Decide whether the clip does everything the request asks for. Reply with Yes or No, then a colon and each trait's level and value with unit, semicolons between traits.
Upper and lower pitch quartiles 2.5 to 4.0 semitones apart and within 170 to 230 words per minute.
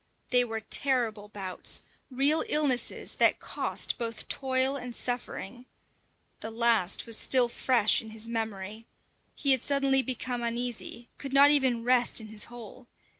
No: average, 2.8 semitones; average, 145 wpm